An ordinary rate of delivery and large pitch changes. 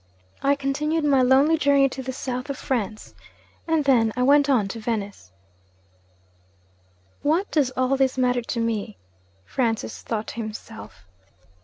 No: average, 145 wpm; average, 3.7 semitones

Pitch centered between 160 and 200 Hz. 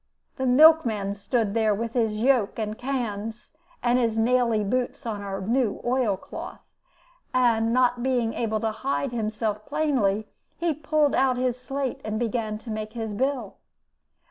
No: high, 235 Hz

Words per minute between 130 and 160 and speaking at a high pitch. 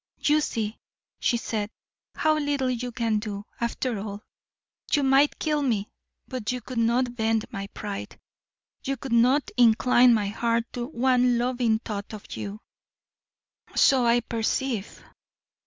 Yes: average, 140 wpm; high, 235 Hz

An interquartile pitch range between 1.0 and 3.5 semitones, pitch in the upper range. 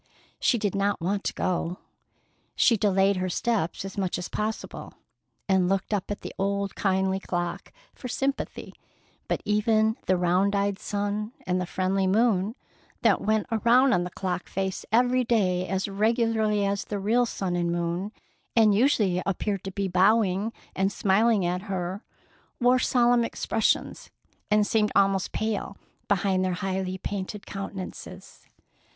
Yes: narrow, 2.6 semitones; high, 200 Hz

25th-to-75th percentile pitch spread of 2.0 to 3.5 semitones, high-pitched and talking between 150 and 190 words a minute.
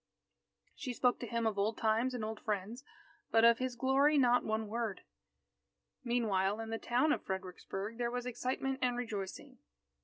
Yes: narrow, 2.5 semitones; high, 235 Hz; average, 165 wpm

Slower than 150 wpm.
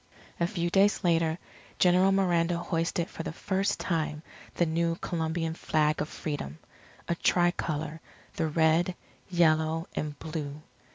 Yes: slow, 135 wpm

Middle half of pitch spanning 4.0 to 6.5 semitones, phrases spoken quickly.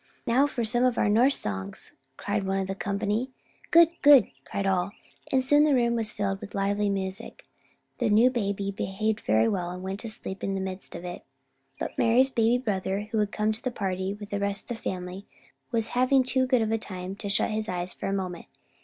No: average, 3.6 semitones; fast, 220 wpm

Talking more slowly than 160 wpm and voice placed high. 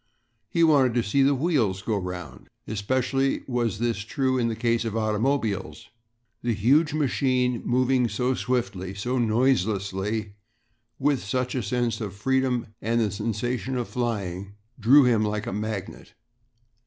No: average, 145 wpm; low, 120 Hz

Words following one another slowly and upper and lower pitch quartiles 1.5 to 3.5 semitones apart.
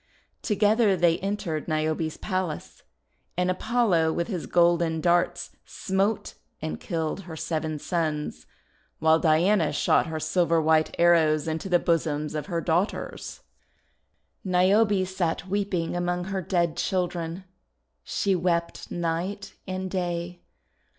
Yes: slow, 120 wpm; average, 2.7 semitones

